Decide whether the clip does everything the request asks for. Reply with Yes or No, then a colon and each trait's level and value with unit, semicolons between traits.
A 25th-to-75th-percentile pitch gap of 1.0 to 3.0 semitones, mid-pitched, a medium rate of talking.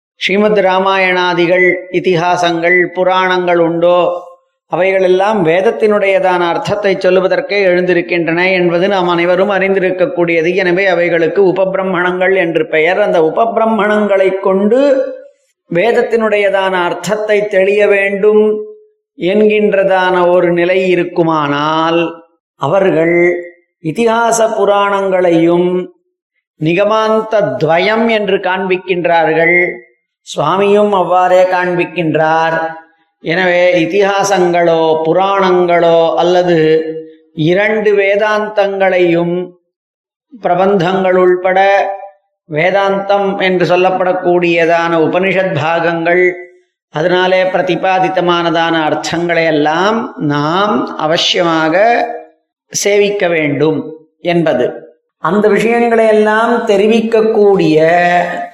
No: narrow, 2.5 semitones; medium, 180 Hz; slow, 65 wpm